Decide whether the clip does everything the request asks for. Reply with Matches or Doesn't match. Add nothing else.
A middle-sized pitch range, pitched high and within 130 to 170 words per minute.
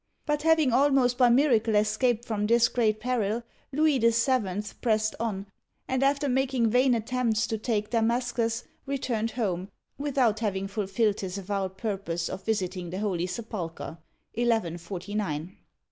Matches